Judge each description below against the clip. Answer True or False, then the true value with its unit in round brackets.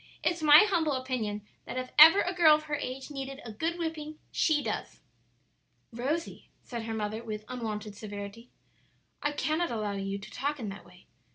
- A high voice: True (255 Hz)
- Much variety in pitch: True (6.2 semitones)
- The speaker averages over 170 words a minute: True (180 wpm)